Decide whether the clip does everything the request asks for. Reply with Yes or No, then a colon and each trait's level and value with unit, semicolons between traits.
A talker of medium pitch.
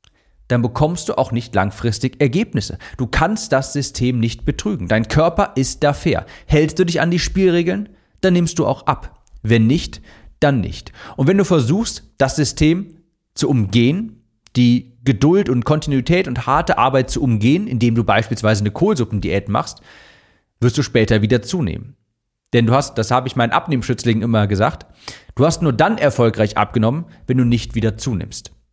No: low, 125 Hz